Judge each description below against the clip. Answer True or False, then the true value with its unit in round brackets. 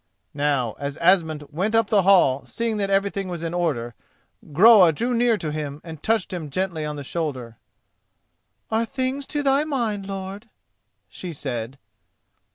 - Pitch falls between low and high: True (180 Hz)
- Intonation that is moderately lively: False (6.8 semitones)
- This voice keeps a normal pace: True (160 wpm)